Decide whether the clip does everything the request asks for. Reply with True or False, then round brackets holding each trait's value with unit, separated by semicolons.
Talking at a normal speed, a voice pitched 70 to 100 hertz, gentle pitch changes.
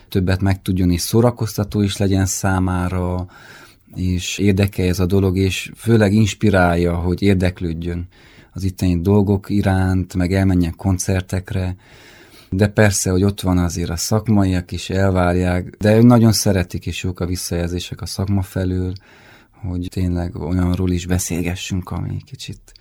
True (135 wpm; 95 Hz; 2.0 semitones)